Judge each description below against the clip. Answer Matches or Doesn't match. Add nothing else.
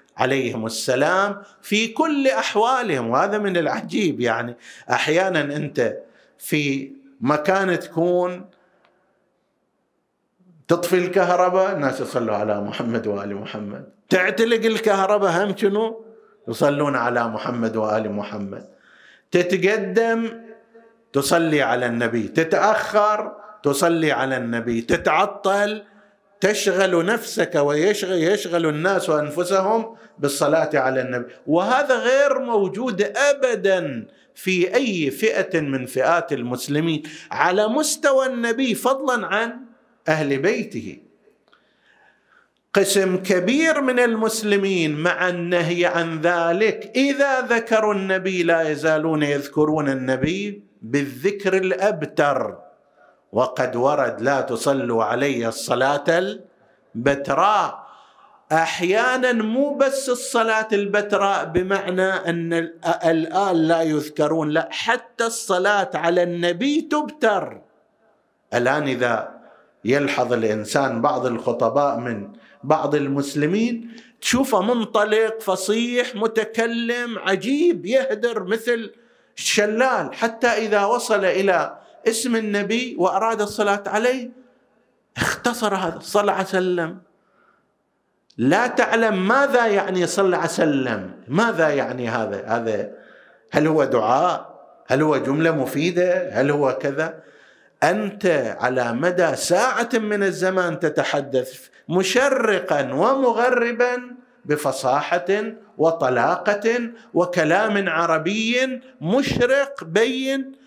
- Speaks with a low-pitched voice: Doesn't match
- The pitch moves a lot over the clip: Matches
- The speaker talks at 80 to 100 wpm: Matches